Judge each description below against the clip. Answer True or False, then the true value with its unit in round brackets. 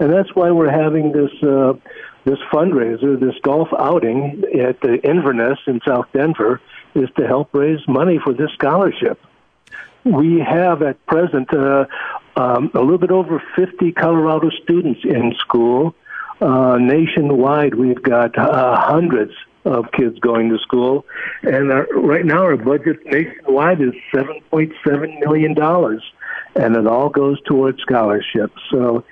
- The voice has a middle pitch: True (145 Hz)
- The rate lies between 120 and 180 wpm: True (150 wpm)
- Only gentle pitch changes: False (3.3 semitones)